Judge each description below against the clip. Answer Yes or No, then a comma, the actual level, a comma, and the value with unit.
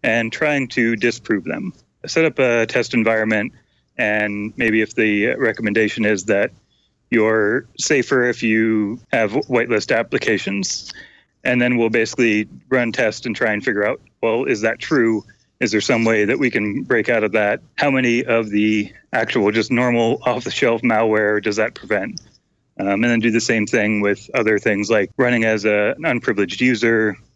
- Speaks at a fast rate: No, average, 180 wpm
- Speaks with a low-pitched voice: Yes, low, 110 Hz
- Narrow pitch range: Yes, narrow, 2.0 semitones